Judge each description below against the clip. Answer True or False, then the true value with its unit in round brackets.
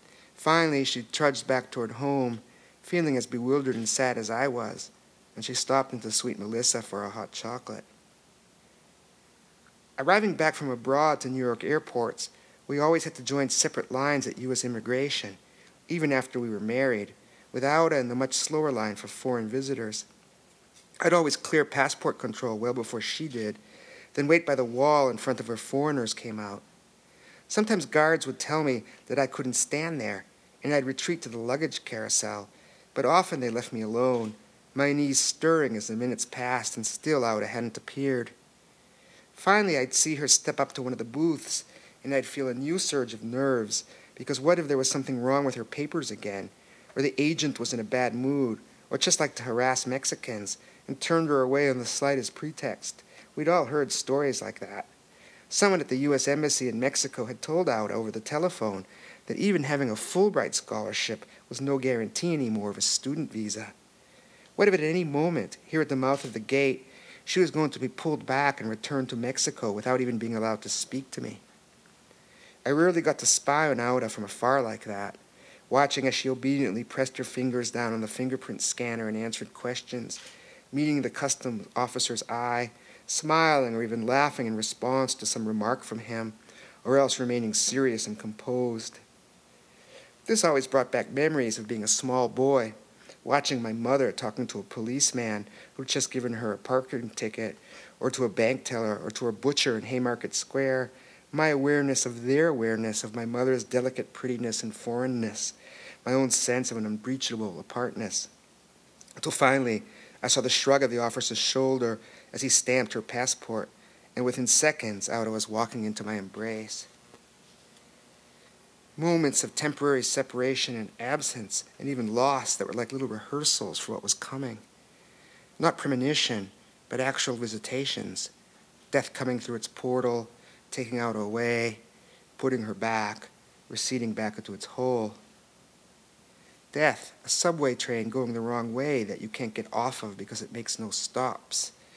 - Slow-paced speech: False (175 wpm)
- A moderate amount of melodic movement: True (3.3 semitones)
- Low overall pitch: True (125 Hz)